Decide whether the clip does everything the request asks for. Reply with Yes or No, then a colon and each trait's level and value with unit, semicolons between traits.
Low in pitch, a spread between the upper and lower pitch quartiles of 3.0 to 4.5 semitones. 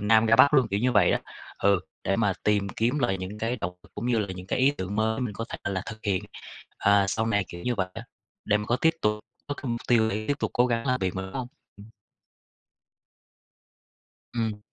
Yes: low, 110 Hz; average, 3.3 semitones